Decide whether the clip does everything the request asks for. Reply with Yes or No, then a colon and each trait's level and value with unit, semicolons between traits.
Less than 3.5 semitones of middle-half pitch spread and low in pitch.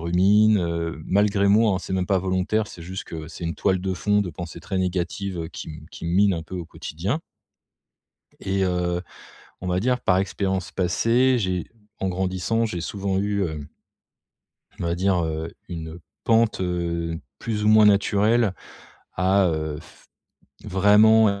Yes: average, 3.0 semitones; very low, 95 Hz